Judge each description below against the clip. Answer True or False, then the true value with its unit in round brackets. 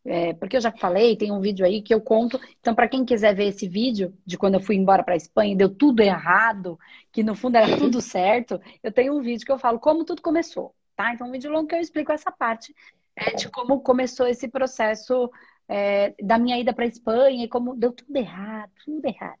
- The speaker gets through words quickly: True (230 wpm)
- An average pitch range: True (4.2 semitones)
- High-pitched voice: True (235 Hz)